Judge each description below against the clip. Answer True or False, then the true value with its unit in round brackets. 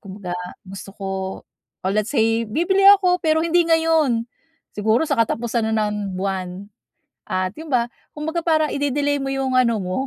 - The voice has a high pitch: True (235 Hz)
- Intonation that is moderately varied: False (7.3 semitones)